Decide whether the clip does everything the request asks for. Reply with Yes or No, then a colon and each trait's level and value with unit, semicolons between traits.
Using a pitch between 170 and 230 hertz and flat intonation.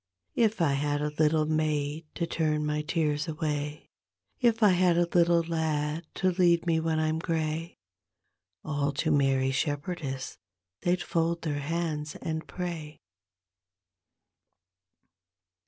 No: medium, 155 Hz; narrow, 2.2 semitones